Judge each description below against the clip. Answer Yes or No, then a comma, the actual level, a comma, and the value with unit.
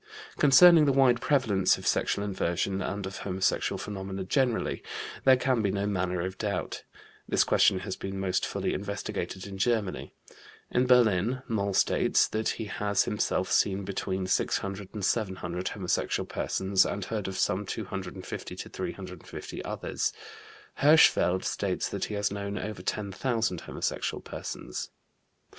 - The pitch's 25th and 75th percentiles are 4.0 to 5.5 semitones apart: No, average, 2.9 semitones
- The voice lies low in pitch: Yes, low, 100 Hz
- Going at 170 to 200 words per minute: No, average, 145 wpm